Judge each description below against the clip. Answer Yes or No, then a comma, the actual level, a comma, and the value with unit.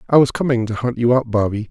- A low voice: Yes, low, 120 Hz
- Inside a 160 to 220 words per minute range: No, fast, 280 wpm